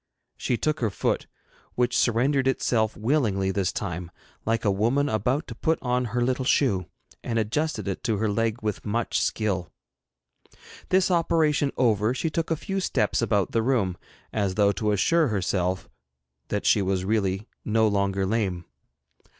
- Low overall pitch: Yes, low, 110 Hz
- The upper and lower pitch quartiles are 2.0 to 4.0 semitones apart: No, average, 4.8 semitones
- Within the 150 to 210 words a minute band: Yes, average, 160 wpm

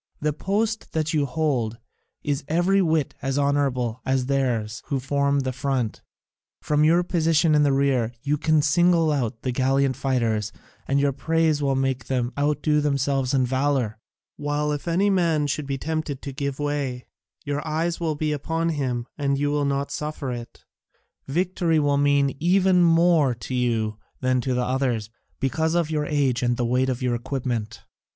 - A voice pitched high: No, medium, 140 Hz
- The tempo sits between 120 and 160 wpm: No, average, 175 wpm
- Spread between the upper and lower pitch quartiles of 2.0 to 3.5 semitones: Yes, average, 3.2 semitones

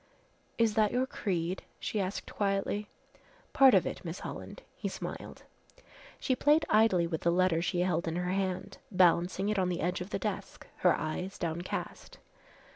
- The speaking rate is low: No, average, 170 wpm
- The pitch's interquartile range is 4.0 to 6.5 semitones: No, average, 3.0 semitones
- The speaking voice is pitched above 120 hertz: Yes, medium, 185 Hz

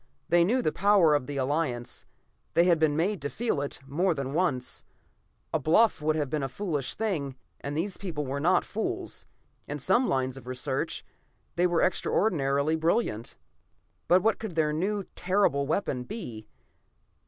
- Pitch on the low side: No, medium, 155 Hz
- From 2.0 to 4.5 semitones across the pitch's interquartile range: No, average, 5.0 semitones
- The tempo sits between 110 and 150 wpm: No, average, 165 wpm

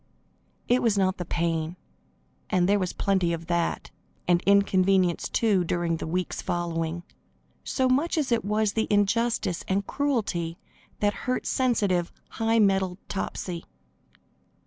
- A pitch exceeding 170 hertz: Yes, high, 190 Hz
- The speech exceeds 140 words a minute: No, slow, 135 wpm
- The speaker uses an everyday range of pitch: Yes, average, 4.1 semitones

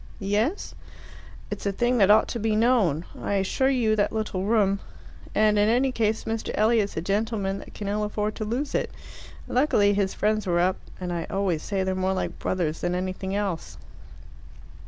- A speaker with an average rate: Yes, average, 185 wpm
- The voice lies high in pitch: Yes, high, 205 Hz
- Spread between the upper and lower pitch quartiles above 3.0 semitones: No, average, 2.7 semitones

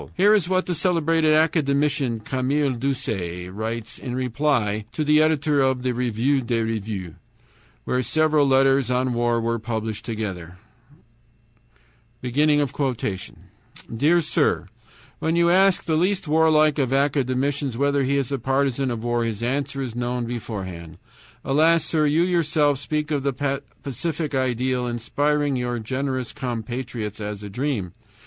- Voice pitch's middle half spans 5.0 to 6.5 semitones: No, average, 4.1 semitones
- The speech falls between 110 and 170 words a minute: Yes, average, 140 wpm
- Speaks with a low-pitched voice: Yes, low, 130 Hz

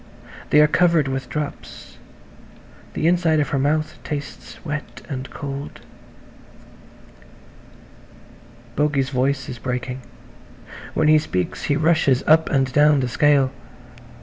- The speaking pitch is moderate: Yes, medium, 145 Hz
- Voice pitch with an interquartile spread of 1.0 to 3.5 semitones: Yes, narrow, 2.4 semitones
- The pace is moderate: No, slow, 120 wpm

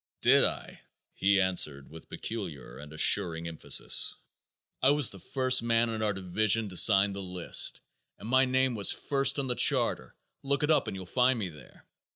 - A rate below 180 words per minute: No, average, 185 wpm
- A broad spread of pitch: Yes, wide, 6.3 semitones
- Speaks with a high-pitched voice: No, low, 105 Hz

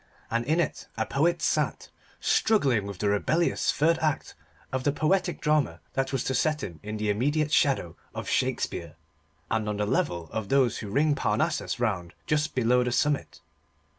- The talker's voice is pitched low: Yes, low, 130 Hz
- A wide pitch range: Yes, wide, 6.2 semitones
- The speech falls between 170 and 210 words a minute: Yes, average, 175 wpm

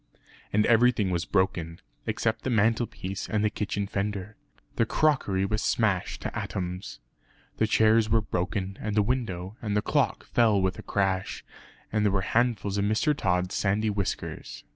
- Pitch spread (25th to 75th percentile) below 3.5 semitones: Yes, narrow, 2.6 semitones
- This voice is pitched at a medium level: No, low, 105 Hz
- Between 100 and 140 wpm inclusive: No, average, 165 wpm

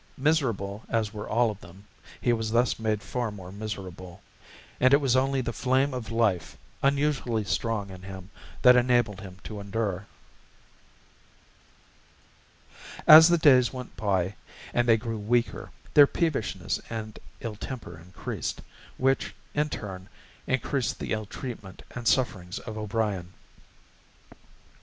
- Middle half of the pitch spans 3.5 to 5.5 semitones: Yes, average, 4.1 semitones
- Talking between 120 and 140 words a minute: Yes, slow, 135 wpm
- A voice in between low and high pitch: No, low, 110 Hz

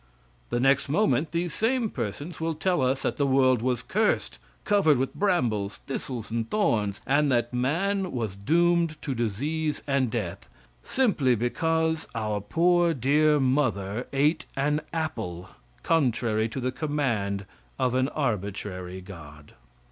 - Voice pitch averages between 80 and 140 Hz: Yes, low, 135 Hz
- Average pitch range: No, wide, 6.4 semitones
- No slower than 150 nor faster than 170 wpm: No, average, 140 wpm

